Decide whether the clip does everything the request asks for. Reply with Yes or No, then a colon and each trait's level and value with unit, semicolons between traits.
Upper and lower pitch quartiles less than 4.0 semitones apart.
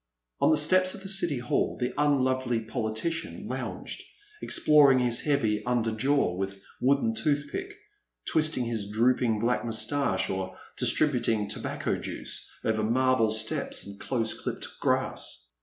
No: average, 4.7 semitones